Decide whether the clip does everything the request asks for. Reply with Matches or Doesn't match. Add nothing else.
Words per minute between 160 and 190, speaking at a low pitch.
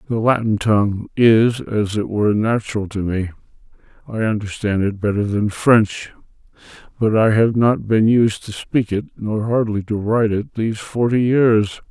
Matches